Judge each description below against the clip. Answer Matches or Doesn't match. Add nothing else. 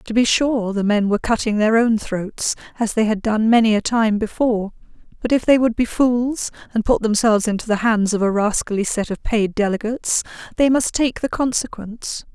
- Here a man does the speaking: Doesn't match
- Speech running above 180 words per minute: Matches